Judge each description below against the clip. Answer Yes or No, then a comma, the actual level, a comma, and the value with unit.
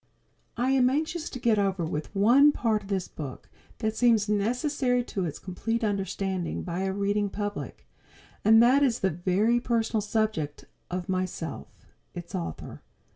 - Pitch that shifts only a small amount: No, average, 4.1 semitones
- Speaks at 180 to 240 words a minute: No, average, 155 wpm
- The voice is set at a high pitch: Yes, high, 210 Hz